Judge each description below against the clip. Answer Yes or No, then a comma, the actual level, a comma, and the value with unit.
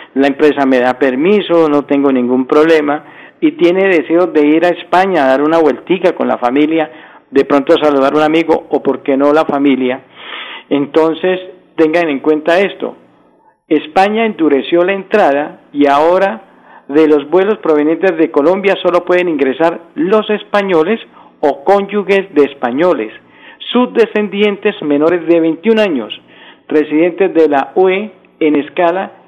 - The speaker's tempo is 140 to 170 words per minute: Yes, average, 150 wpm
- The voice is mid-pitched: Yes, medium, 160 Hz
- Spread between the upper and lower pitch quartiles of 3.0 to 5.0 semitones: Yes, average, 4.5 semitones